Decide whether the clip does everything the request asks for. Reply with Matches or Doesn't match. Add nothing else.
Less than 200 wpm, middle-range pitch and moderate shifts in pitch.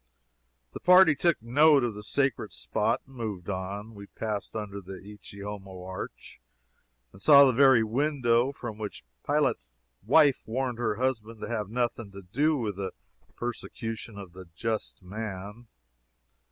Doesn't match